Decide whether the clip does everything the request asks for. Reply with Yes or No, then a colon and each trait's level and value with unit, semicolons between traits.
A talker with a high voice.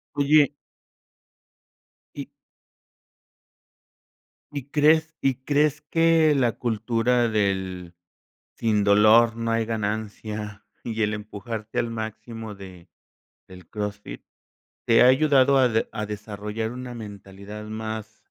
No: low, 110 Hz